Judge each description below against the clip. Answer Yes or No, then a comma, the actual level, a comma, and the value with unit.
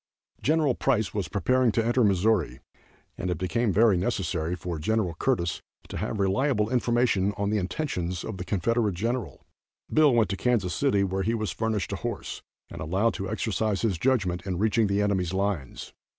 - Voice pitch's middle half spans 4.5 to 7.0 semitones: No, average, 4.0 semitones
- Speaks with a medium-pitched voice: No, low, 105 Hz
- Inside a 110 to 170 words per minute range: No, average, 180 wpm